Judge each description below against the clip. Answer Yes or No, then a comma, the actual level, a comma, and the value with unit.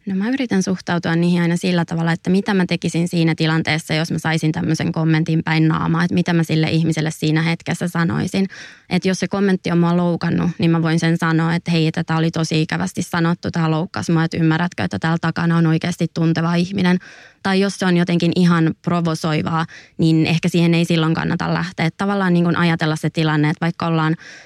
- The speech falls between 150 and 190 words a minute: No, fast, 205 wpm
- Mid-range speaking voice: Yes, medium, 165 Hz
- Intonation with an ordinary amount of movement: No, narrow, 1.4 semitones